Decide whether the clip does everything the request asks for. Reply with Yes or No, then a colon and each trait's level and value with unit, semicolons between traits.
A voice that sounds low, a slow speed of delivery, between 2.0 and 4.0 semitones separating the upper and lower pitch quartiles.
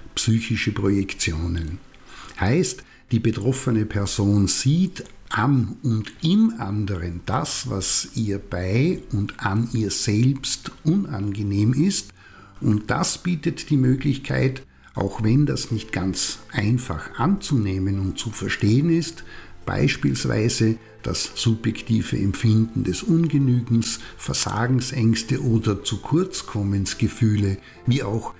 No: low, 115 Hz; slow, 105 wpm; average, 4.6 semitones